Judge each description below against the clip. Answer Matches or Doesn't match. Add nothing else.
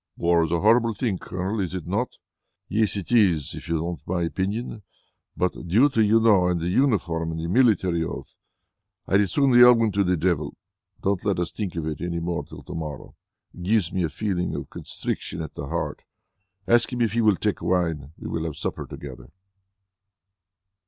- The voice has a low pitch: Matches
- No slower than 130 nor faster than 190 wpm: Doesn't match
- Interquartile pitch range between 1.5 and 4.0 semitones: Doesn't match